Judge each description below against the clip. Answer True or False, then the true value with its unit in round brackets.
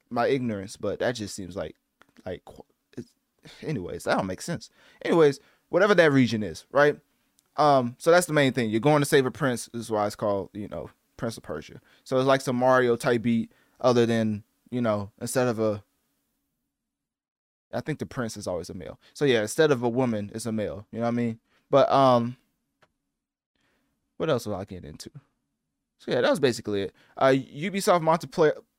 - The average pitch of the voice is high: False (120 Hz)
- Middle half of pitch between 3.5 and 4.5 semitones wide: True (4.0 semitones)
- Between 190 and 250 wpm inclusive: True (200 wpm)